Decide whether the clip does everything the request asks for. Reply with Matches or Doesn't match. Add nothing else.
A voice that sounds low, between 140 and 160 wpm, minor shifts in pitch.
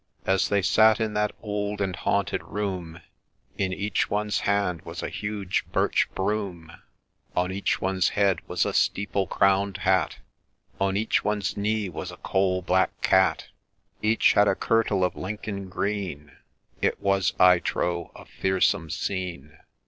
Matches